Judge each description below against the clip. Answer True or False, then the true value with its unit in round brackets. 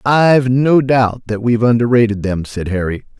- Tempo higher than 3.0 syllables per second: True (5.1 syllables/s)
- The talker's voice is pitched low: True (115 Hz)